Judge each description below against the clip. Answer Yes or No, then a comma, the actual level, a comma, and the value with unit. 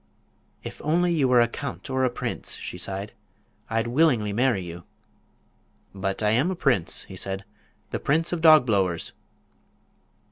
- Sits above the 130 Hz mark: No, low, 120 Hz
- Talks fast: No, average, 150 wpm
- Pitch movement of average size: No, wide, 7.0 semitones